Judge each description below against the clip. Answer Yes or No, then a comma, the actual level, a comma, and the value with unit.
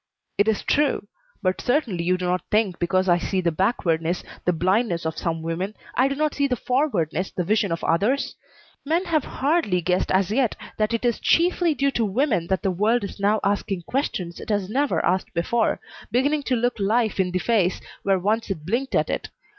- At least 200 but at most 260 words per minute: Yes, fast, 205 wpm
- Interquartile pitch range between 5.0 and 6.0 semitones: Yes, wide, 5.5 semitones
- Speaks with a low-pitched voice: No, high, 205 Hz